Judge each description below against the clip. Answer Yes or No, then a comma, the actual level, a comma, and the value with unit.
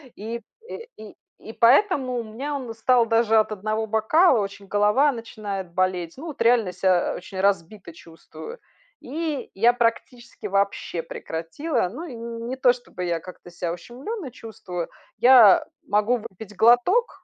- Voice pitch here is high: Yes, high, 225 Hz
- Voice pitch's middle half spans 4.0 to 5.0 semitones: Yes, average, 4.4 semitones